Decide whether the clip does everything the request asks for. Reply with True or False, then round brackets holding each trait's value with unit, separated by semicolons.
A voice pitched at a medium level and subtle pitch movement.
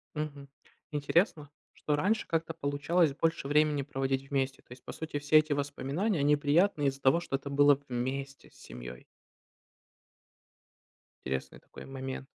True (145 Hz; 2.2 semitones)